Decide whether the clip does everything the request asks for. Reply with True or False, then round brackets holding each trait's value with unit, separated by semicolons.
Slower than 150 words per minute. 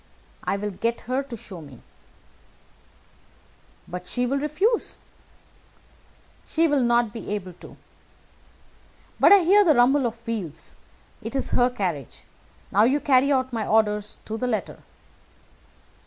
True (135 wpm)